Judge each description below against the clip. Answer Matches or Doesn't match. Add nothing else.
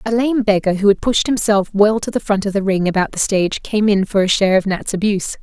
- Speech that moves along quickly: Matches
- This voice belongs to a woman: Matches